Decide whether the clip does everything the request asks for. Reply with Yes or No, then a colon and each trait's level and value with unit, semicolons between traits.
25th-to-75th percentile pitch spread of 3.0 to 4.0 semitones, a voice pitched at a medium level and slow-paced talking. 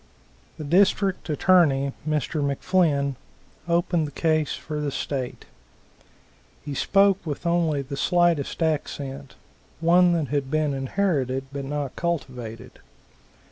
Yes: average, 3.7 semitones; medium, 150 Hz; slow, 115 wpm